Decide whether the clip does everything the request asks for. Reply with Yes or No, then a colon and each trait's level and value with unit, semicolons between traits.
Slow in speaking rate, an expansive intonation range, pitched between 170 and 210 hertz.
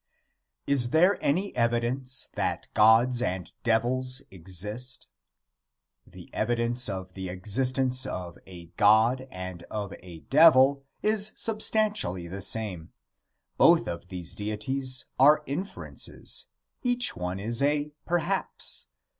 No: slow, 115 wpm; wide, 6.4 semitones; low, 120 Hz